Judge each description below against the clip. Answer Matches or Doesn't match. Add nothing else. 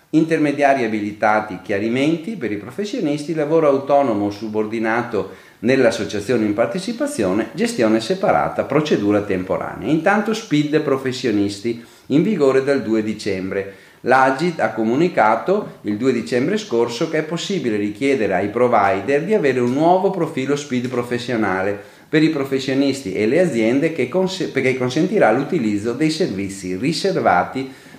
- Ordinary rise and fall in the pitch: Doesn't match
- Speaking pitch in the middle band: Doesn't match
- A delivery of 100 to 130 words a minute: Matches